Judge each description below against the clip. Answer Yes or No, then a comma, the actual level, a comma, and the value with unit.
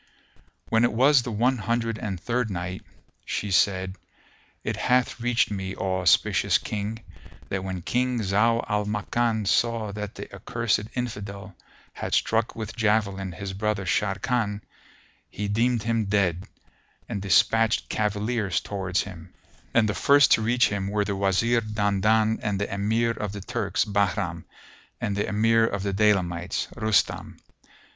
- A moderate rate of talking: Yes, average, 150 wpm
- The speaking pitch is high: No, low, 105 Hz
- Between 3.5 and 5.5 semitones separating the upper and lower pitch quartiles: No, narrow, 2.6 semitones